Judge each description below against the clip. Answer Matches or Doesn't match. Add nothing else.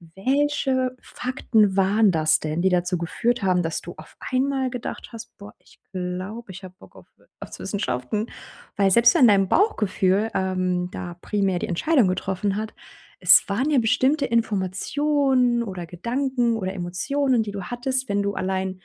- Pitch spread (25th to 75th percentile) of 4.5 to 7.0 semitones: Matches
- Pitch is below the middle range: Doesn't match